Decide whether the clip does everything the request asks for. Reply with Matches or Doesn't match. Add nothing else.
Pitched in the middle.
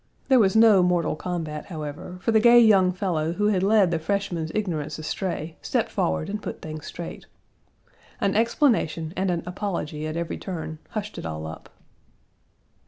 Matches